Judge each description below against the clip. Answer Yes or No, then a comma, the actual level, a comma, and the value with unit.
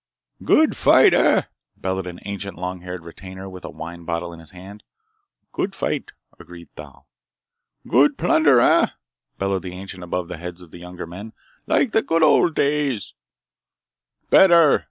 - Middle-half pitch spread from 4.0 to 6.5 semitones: Yes, wide, 5.4 semitones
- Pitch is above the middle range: No, very low, 95 Hz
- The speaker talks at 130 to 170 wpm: Yes, average, 155 wpm